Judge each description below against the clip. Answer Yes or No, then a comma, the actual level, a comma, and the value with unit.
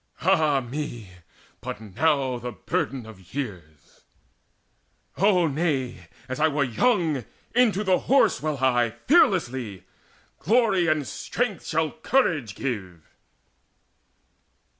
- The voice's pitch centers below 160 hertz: Yes, medium, 140 Hz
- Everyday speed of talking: No, slow, 105 wpm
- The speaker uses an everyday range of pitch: No, wide, 7.0 semitones